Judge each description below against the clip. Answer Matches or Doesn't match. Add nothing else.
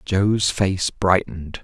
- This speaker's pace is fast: Doesn't match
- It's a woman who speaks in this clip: Doesn't match